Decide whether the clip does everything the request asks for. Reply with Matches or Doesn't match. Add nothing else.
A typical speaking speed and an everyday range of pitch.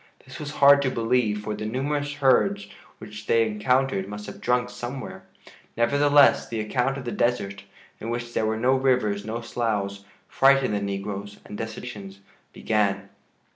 Matches